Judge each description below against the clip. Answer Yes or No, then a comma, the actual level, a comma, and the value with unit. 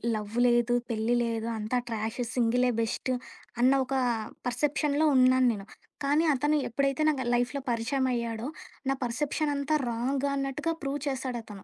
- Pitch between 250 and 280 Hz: Yes, very high, 255 Hz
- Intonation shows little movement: No, average, 3.2 semitones